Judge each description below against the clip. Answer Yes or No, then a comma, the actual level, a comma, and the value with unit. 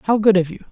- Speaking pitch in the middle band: No, high, 195 Hz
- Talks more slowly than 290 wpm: No, fast, 335 wpm